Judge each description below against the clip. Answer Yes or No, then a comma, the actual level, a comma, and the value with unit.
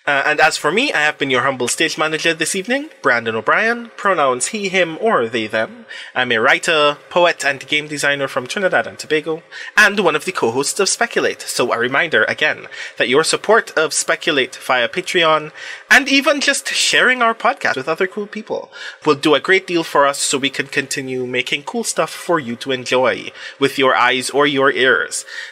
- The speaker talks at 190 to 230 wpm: Yes, average, 200 wpm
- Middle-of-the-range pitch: Yes, medium, 160 Hz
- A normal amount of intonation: No, wide, 7.1 semitones